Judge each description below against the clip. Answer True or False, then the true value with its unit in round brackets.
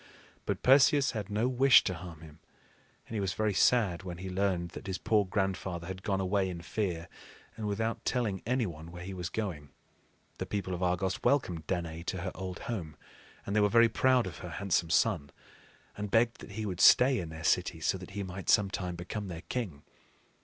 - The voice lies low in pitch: True (95 Hz)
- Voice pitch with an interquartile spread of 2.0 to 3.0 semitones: False (3.6 semitones)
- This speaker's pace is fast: True (210 wpm)